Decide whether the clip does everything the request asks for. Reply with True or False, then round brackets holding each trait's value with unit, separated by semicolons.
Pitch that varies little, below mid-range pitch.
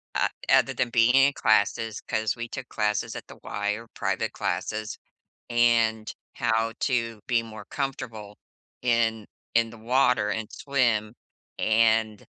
True (1.5 semitones; 115 Hz)